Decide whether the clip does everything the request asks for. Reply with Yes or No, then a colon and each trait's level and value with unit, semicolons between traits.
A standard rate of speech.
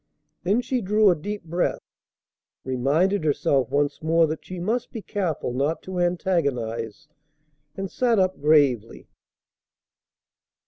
No: slow, 125 wpm